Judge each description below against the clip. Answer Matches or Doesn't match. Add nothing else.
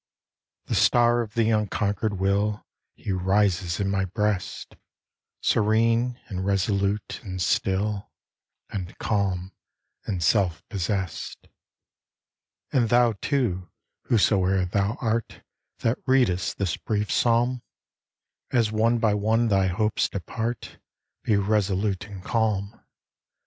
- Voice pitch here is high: Doesn't match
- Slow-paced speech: Matches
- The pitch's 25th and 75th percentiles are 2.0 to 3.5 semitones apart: Matches